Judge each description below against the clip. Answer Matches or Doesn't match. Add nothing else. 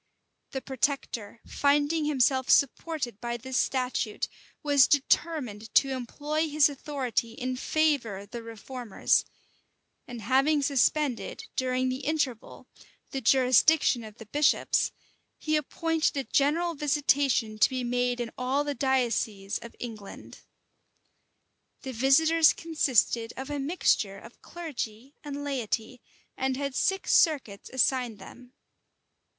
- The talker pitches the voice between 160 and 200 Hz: Doesn't match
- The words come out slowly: Matches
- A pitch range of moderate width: Matches